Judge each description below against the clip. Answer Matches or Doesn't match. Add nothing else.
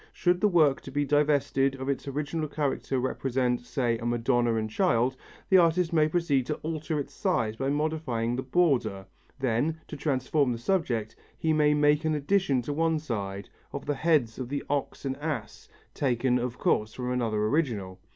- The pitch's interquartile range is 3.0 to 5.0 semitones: Matches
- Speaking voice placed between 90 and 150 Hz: Matches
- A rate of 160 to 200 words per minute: Matches